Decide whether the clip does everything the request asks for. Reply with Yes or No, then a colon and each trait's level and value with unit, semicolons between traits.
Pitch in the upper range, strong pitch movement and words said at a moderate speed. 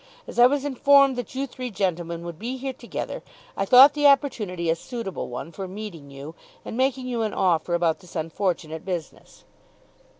Yes: high, 200 Hz; wide, 7.2 semitones; average, 180 wpm